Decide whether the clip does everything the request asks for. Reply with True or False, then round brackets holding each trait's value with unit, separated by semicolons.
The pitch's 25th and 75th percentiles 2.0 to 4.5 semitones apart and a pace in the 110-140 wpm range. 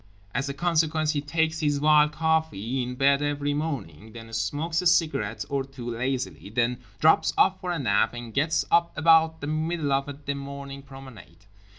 False (4.2 semitones; 180 wpm)